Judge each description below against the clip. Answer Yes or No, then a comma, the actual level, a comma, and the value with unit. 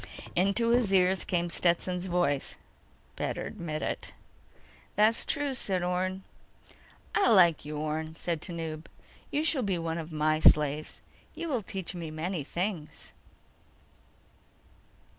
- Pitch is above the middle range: No, medium, 175 Hz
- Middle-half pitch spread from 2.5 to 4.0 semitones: Yes, average, 3.6 semitones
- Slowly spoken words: Yes, slow, 125 wpm